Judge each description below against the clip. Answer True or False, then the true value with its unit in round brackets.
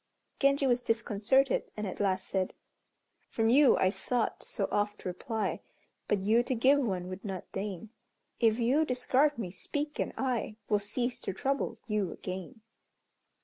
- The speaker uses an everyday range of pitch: True (4.6 semitones)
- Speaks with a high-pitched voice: True (225 Hz)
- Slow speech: False (155 wpm)